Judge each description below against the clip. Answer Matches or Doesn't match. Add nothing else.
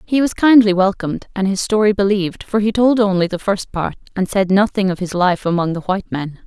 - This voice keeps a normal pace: Doesn't match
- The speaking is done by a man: Doesn't match